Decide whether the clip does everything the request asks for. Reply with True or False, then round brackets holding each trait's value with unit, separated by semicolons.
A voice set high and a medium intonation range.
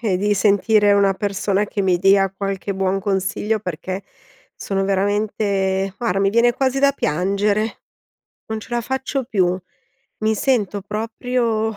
False (205 Hz; 2.3 semitones)